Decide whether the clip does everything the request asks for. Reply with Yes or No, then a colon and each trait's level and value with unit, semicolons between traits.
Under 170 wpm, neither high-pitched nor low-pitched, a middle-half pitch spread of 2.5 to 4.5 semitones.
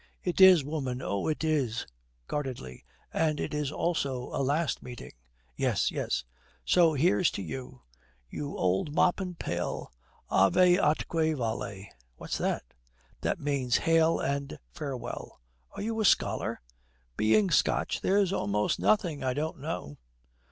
No: slow, 135 wpm; medium, 145 Hz; average, 5.0 semitones